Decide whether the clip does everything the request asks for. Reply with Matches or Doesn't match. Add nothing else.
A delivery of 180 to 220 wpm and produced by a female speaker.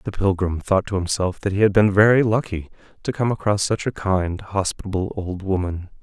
Doesn't match